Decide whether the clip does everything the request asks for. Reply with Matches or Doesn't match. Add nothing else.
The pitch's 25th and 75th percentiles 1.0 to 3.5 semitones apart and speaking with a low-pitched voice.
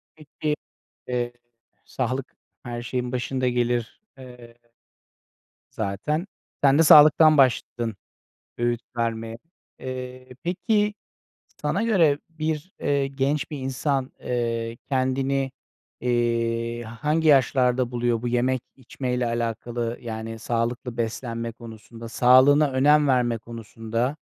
Matches